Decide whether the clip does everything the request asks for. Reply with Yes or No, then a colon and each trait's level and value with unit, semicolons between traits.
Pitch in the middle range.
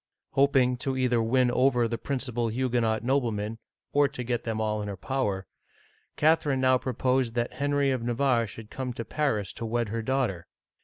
No: low, 120 Hz